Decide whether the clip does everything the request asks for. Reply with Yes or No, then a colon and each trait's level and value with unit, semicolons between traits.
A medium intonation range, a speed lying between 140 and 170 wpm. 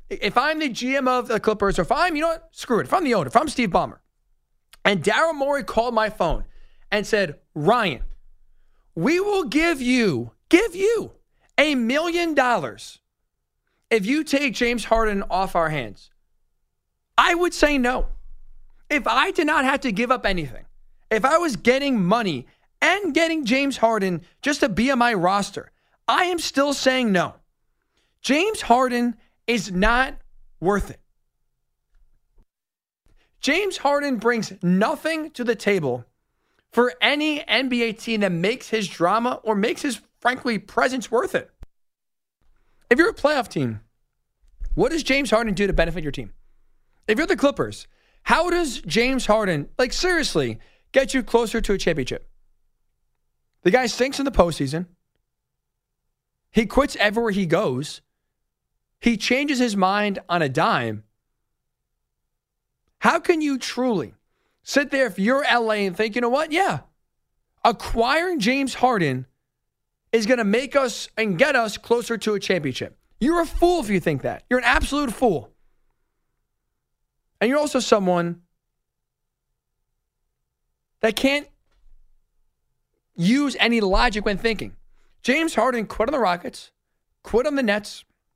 No: wide, 6.9 semitones; average, 150 wpm